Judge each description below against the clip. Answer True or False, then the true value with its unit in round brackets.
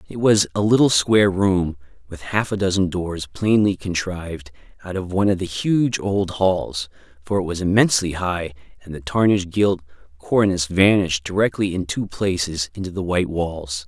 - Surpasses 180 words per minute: False (175 wpm)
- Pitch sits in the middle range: False (90 Hz)